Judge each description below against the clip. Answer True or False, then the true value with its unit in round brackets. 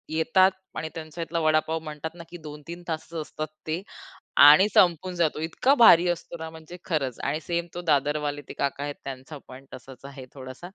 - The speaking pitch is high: False (155 Hz)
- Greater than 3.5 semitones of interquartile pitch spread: False (2.7 semitones)